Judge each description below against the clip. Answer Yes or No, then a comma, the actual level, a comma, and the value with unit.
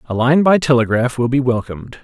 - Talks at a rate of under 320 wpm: Yes, fast, 205 wpm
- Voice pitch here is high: No, low, 130 Hz